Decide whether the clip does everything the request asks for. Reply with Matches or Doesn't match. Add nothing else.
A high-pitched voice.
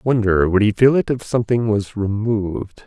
Doesn't match